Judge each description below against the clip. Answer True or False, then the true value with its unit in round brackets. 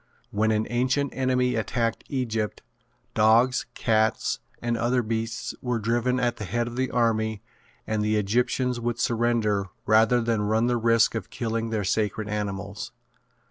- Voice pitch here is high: False (115 Hz)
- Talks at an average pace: True (150 wpm)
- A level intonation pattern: True (1.9 semitones)